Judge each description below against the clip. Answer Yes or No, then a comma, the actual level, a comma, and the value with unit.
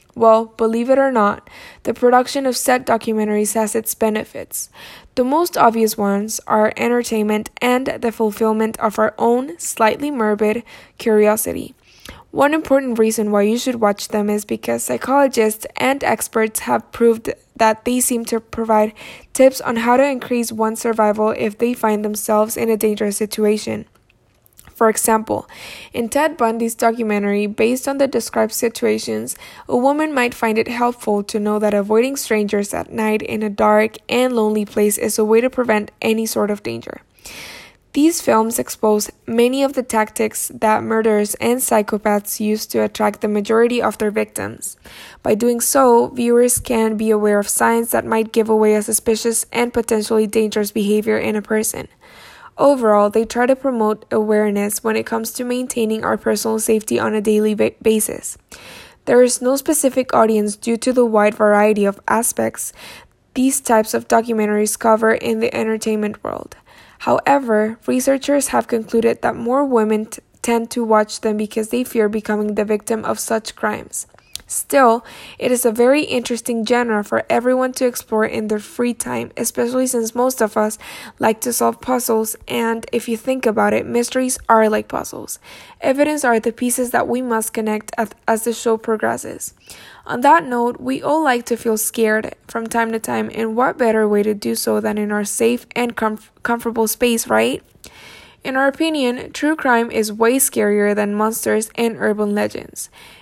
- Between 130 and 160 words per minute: No, average, 170 wpm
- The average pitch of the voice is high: Yes, high, 225 Hz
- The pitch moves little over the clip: Yes, narrow, 2.2 semitones